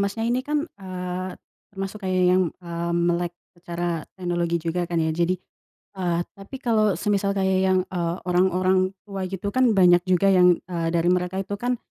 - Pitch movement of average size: No, narrow, 2.2 semitones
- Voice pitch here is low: No, medium, 185 Hz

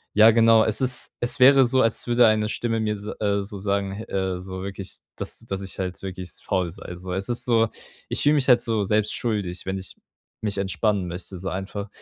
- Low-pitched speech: Yes, low, 100 Hz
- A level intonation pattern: No, average, 3.1 semitones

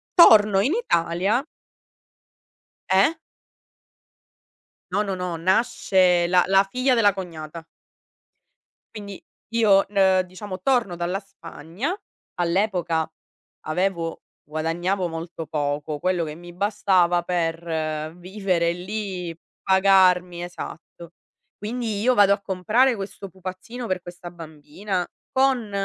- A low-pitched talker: No, medium, 185 Hz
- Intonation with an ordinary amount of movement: Yes, average, 3.1 semitones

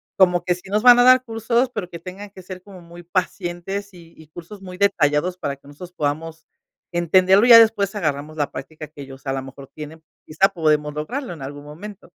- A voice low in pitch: No, medium, 175 Hz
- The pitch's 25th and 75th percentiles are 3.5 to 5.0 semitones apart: Yes, average, 4.6 semitones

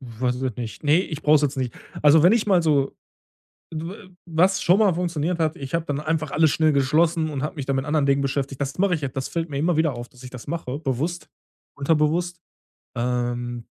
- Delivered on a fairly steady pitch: No, average, 3.8 semitones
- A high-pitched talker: No, medium, 150 Hz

